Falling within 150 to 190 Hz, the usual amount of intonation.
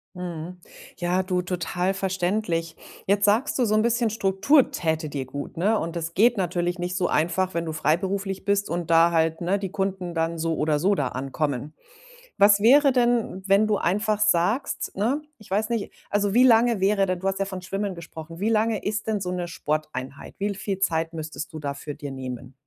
Yes: medium, 185 Hz; average, 3.8 semitones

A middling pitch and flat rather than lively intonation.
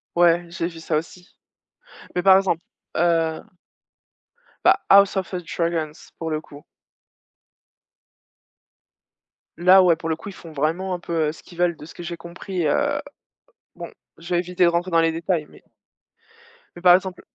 Yes: medium, 170 Hz; narrow, 1.8 semitones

